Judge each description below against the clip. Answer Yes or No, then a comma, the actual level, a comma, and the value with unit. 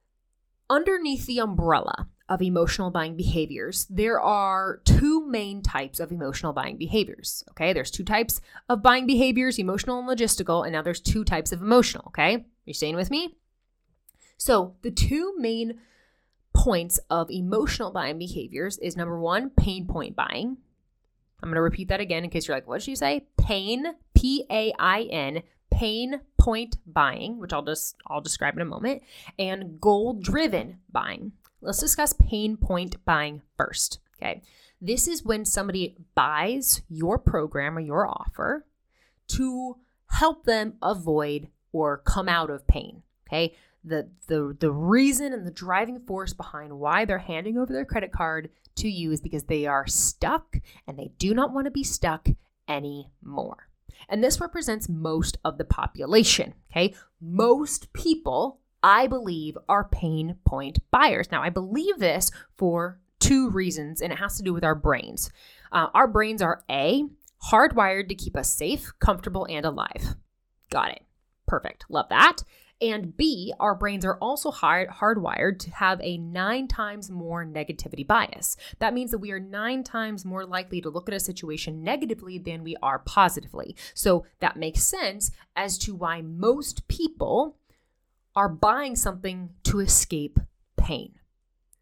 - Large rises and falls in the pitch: Yes, wide, 6.2 semitones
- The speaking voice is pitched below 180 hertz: No, high, 190 Hz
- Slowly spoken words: No, average, 160 wpm